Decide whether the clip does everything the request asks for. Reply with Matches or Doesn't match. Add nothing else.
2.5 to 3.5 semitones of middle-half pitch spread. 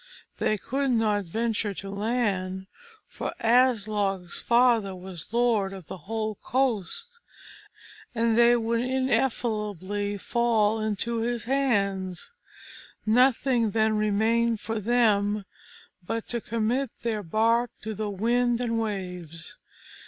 Matches